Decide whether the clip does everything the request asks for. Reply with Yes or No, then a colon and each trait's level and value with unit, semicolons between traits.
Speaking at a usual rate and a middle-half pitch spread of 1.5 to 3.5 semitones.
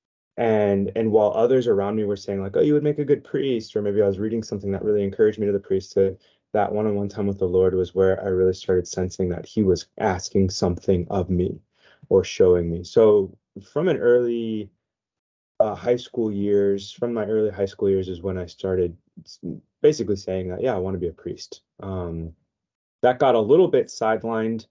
No: fast, 210 wpm; average, 2.7 semitones